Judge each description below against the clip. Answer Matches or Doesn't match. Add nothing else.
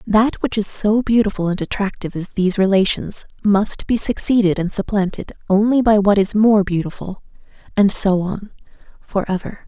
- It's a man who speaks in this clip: Doesn't match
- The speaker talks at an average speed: Matches